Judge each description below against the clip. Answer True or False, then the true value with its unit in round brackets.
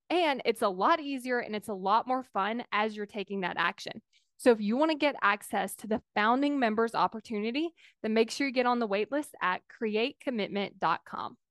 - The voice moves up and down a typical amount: True (4.2 semitones)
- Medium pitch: False (225 Hz)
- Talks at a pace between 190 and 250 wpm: True (200 wpm)